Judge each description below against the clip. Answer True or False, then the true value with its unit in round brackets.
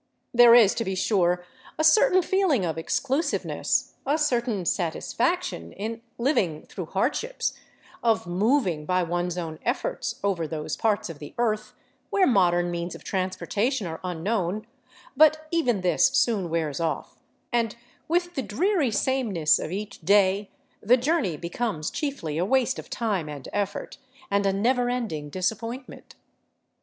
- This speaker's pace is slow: False (150 wpm)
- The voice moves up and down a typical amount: False (6.3 semitones)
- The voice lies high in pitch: True (205 Hz)